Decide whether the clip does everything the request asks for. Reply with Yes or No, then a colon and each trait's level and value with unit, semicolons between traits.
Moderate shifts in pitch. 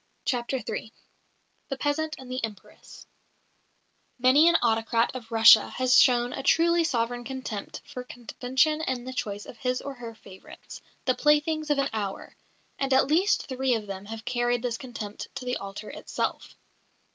Yes: average, 3.0 semitones